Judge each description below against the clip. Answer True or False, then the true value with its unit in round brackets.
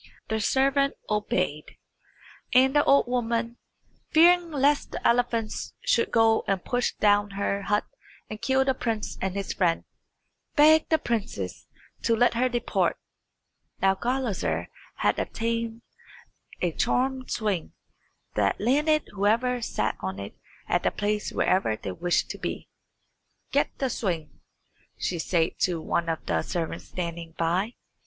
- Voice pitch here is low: False (220 Hz)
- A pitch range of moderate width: False (5.7 semitones)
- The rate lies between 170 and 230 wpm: False (140 wpm)